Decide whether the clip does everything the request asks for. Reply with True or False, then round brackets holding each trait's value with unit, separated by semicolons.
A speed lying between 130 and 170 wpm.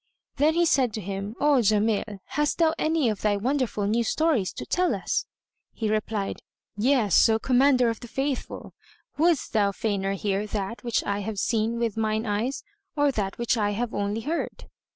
False (180 wpm)